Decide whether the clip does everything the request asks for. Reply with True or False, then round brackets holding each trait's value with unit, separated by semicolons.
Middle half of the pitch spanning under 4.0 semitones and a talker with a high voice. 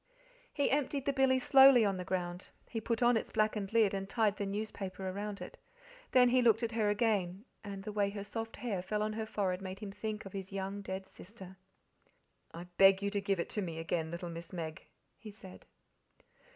True (2.8 semitones; 200 Hz)